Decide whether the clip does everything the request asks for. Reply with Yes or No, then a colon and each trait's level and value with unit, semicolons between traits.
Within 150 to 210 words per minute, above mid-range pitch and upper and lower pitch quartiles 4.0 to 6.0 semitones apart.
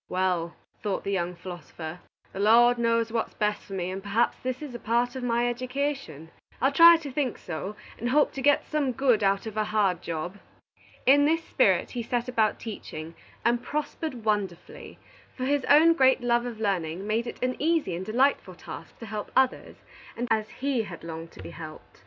Yes: average, 195 wpm; high, 230 Hz; average, 5.3 semitones